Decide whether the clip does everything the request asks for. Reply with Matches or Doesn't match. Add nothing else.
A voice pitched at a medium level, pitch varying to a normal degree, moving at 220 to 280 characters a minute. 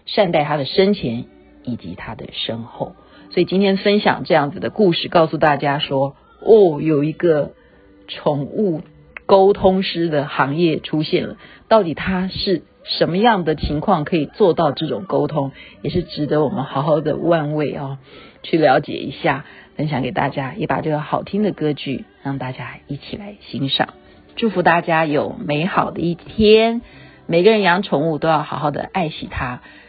Matches